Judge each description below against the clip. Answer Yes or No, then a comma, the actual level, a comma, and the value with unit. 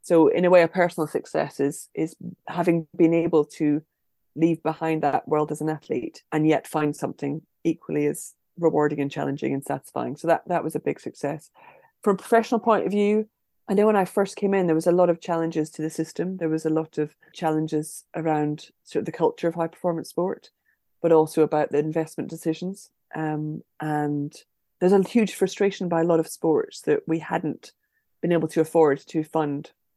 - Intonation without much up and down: No, average, 3.1 semitones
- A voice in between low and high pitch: Yes, medium, 160 Hz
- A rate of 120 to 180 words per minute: No, average, 200 wpm